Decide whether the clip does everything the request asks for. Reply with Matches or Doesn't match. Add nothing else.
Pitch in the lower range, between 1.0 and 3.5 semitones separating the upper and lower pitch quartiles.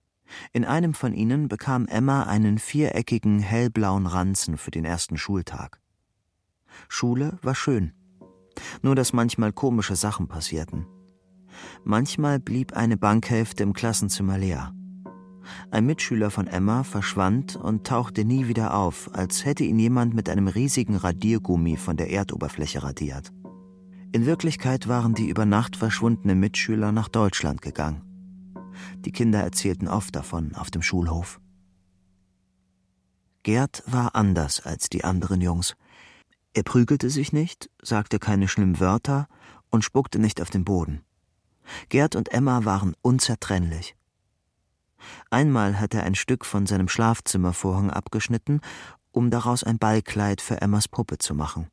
Doesn't match